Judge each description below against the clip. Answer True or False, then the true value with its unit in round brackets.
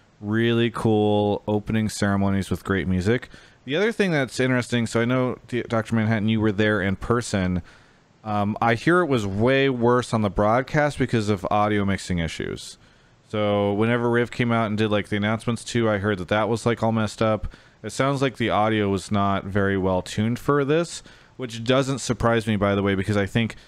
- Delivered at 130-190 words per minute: False (200 wpm)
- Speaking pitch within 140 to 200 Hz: False (110 Hz)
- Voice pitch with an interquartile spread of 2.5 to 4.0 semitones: True (2.8 semitones)